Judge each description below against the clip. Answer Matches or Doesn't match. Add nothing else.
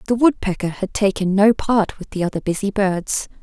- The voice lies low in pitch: Doesn't match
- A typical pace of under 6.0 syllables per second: Matches